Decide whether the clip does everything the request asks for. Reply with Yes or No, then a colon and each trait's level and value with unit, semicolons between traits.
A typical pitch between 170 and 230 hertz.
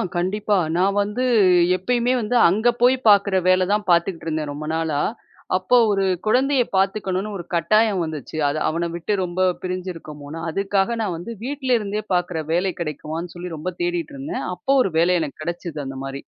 Yes: medium, 185 Hz